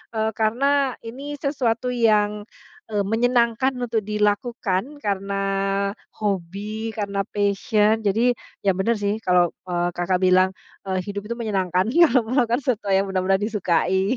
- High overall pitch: Yes, high, 210 Hz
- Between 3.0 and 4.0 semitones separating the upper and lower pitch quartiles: Yes, average, 3.5 semitones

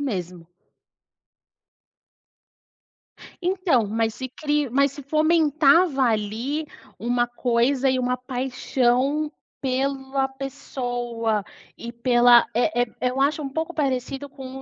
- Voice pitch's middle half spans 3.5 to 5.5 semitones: No, average, 2.7 semitones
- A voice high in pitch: Yes, very high, 260 Hz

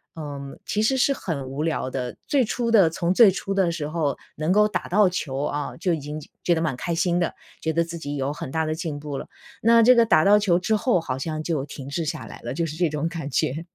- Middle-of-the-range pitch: Yes, medium, 165 Hz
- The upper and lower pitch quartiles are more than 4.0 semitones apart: Yes, average, 4.4 semitones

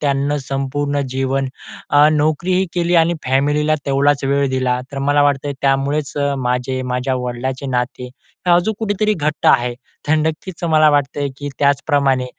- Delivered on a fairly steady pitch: Yes, narrow, 2.0 semitones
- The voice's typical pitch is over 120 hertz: Yes, medium, 140 Hz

